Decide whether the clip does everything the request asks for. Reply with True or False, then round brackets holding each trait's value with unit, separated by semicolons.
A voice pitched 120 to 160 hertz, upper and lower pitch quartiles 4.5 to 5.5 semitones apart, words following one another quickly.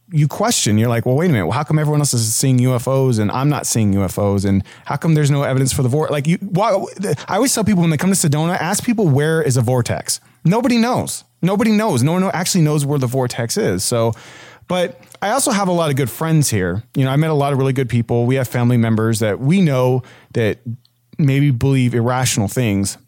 True (135 Hz; 5.2 semitones; 240 wpm)